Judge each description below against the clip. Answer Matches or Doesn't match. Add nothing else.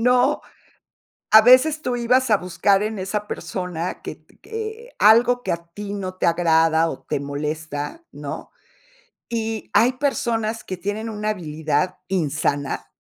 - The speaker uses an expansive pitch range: Matches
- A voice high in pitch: Matches